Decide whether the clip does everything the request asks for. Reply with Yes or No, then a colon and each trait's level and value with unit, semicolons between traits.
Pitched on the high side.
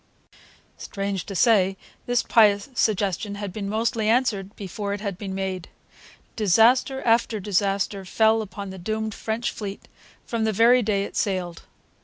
Yes: high, 205 Hz